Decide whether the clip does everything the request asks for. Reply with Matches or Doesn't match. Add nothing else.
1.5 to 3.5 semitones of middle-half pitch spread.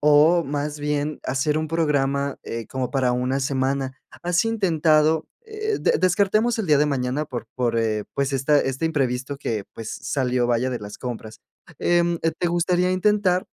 Doesn't match